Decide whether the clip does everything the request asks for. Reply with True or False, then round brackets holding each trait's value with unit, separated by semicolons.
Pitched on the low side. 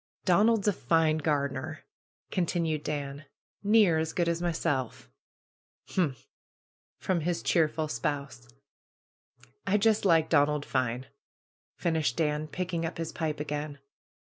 False (160 Hz)